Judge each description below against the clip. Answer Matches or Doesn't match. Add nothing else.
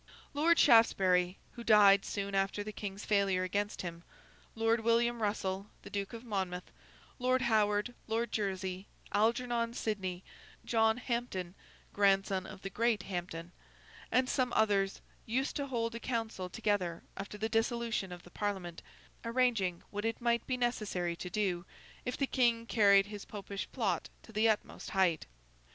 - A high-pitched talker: Matches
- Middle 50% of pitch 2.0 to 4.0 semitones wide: Matches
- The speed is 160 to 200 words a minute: Doesn't match